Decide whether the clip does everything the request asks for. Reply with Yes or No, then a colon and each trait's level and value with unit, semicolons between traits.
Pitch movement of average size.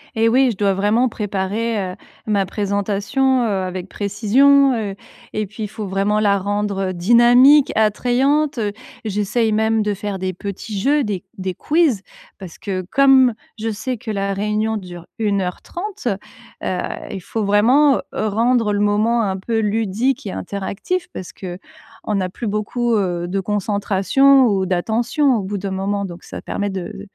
Yes: average, 3.3 semitones